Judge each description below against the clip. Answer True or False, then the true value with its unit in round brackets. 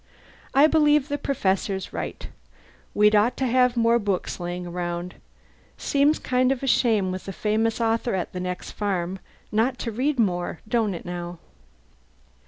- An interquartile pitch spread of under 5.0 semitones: False (5.5 semitones)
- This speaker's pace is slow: False (160 wpm)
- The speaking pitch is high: True (215 Hz)